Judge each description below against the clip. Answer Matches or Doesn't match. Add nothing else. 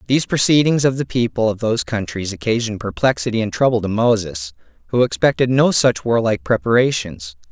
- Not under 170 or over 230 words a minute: Doesn't match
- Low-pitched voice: Matches